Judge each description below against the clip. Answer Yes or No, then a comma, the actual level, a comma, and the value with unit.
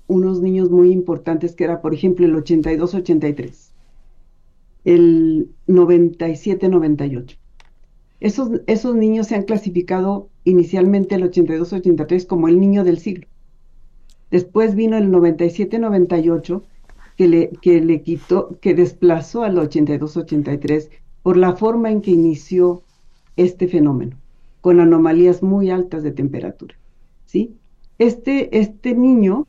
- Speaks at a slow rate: Yes, slow, 115 wpm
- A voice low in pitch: No, medium, 180 Hz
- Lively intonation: No, average, 2.9 semitones